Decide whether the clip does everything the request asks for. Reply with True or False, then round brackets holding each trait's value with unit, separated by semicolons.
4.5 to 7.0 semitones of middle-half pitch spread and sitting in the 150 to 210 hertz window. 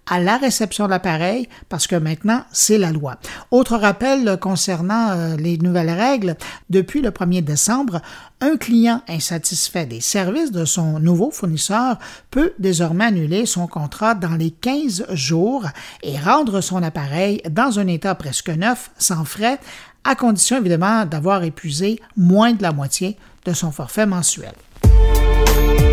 True (5.5 semitones; 185 Hz)